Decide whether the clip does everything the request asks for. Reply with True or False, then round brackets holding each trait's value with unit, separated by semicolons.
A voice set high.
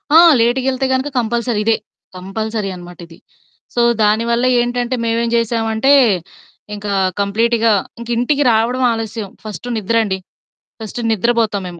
True (230 Hz)